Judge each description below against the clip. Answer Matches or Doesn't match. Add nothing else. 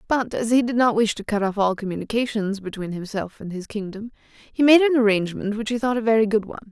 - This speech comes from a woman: Matches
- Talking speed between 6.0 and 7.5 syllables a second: Matches